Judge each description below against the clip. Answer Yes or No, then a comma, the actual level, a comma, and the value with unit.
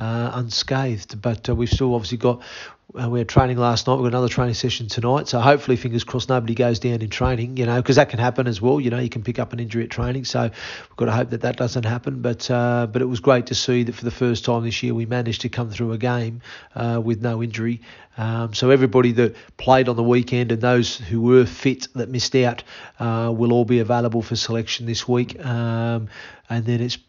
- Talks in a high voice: No, low, 120 Hz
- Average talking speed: No, fast, 245 wpm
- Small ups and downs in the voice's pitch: Yes, narrow, 1.2 semitones